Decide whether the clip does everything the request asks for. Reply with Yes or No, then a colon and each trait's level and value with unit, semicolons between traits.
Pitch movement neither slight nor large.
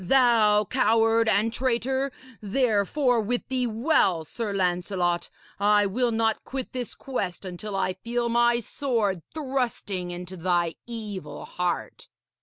Yes: average, 4.4 semitones